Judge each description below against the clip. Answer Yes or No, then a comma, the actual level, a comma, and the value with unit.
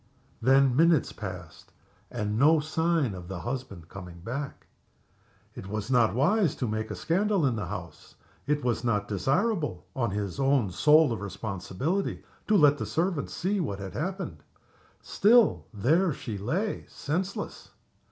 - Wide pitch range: Yes, wide, 7.9 semitones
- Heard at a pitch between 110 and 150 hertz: Yes, low, 135 Hz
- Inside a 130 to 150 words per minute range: Yes, average, 145 wpm